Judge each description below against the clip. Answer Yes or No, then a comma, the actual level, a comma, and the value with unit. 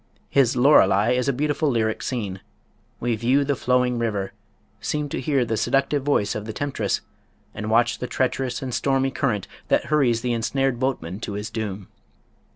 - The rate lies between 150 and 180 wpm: Yes, average, 170 wpm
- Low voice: Yes, low, 125 Hz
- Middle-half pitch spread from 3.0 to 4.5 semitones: Yes, average, 3.6 semitones